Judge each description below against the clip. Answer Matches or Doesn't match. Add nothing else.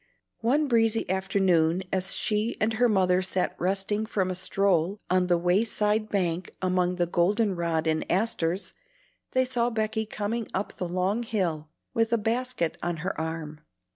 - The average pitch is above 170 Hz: Matches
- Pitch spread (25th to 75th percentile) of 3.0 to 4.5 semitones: Matches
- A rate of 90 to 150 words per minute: Doesn't match